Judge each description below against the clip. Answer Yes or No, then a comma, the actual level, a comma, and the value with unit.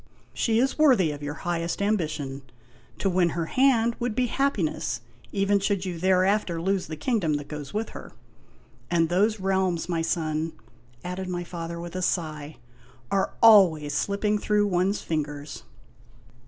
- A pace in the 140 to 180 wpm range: Yes, average, 155 wpm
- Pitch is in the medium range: Yes, medium, 180 Hz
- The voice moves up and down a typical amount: Yes, average, 4.1 semitones